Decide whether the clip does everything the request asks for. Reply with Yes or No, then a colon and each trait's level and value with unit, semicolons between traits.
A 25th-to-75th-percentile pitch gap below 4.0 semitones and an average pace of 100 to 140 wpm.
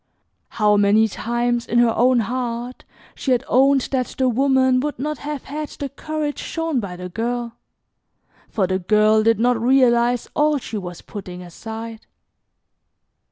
No: average, 3.4 semitones; average, 155 wpm